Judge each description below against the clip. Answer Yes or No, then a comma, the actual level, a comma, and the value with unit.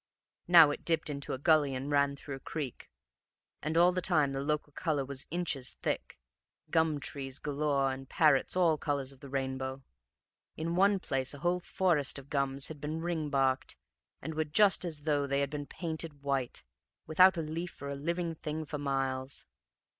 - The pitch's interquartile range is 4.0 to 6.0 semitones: No, average, 2.9 semitones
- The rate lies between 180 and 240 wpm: Yes, average, 185 wpm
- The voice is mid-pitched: Yes, medium, 145 Hz